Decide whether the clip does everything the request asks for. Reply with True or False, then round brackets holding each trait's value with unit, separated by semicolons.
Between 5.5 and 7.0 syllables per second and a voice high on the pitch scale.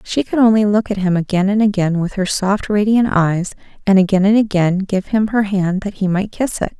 False (5.2 syllables/s; 200 Hz)